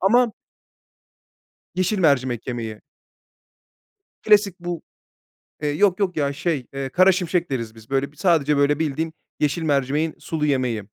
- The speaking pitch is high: No, medium, 150 Hz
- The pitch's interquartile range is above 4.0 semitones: Yes, average, 4.7 semitones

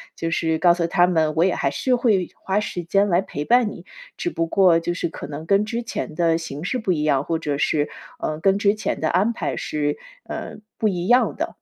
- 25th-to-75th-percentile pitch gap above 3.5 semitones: Yes, average, 4.0 semitones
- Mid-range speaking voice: Yes, medium, 175 Hz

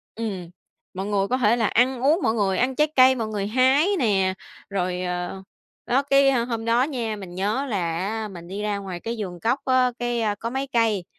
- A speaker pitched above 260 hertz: No, high, 225 Hz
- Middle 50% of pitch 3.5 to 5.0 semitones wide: Yes, average, 4.7 semitones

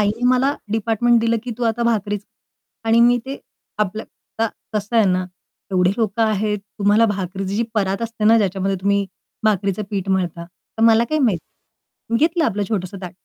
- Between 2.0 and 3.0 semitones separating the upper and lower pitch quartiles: Yes, average, 2.7 semitones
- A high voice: Yes, high, 210 Hz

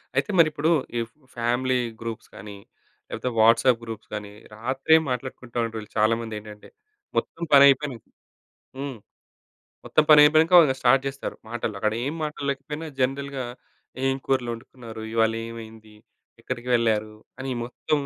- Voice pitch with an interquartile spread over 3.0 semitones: Yes, average, 3.5 semitones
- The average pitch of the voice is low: Yes, low, 125 Hz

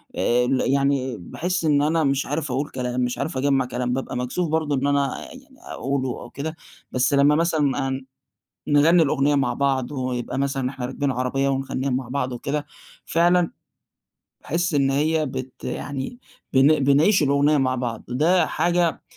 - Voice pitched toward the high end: No, medium, 140 Hz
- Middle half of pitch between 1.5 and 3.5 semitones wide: Yes, average, 2.7 semitones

